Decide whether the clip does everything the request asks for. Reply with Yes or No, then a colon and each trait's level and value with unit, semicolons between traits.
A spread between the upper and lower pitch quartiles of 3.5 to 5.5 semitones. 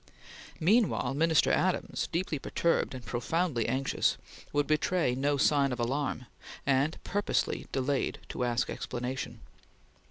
Yes: average, 4.1 semitones